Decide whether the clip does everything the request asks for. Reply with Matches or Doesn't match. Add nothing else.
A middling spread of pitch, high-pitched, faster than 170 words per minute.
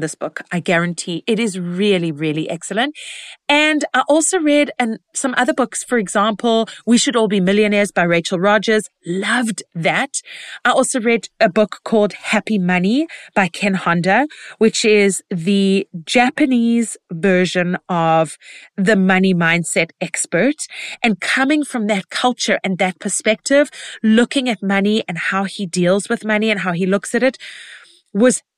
Doesn't match